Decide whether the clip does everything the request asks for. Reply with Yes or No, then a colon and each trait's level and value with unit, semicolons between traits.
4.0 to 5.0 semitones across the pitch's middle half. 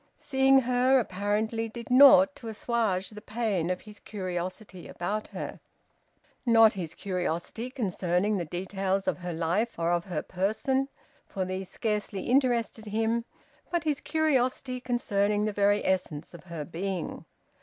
Yes: average, 4.6 semitones